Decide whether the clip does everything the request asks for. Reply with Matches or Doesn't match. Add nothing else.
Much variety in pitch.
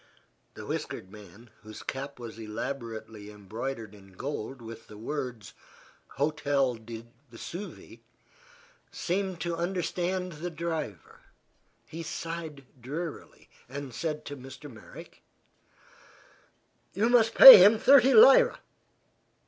Matches